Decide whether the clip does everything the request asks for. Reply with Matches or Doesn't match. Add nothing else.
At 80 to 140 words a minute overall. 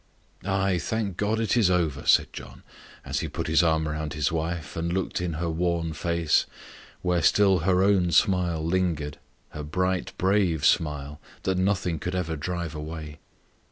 Doesn't match